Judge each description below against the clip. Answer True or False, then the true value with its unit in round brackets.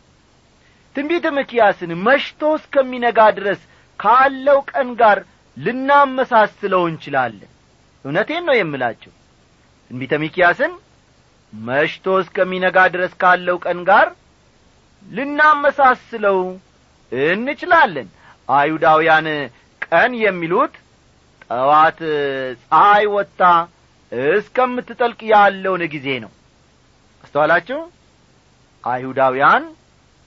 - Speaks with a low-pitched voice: False (190 Hz)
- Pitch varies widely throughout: True (8.5 semitones)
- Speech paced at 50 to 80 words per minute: True (70 wpm)